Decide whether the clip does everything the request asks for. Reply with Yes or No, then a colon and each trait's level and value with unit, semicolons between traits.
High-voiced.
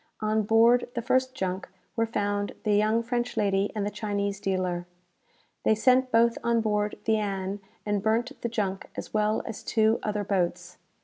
Yes: high, 215 Hz